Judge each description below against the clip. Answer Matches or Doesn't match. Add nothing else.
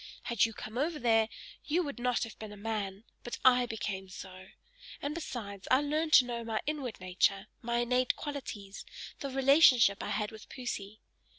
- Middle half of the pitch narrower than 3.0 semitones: Doesn't match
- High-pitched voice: Matches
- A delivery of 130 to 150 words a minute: Doesn't match